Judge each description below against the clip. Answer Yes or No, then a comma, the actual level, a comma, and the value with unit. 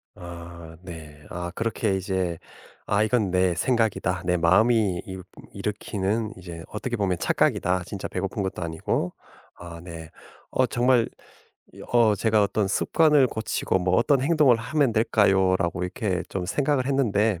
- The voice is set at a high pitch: No, low, 100 Hz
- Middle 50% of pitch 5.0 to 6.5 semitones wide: No, average, 4.3 semitones